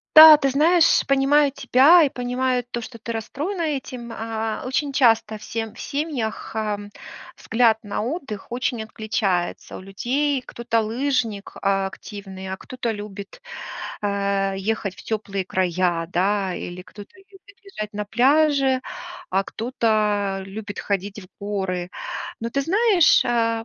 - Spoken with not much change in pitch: No, average, 5.1 semitones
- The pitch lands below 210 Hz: No, high, 225 Hz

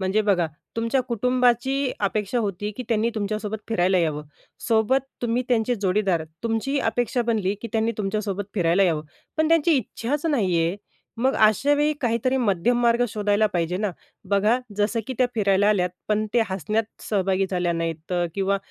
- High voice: Yes, high, 215 Hz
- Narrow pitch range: No, average, 3.8 semitones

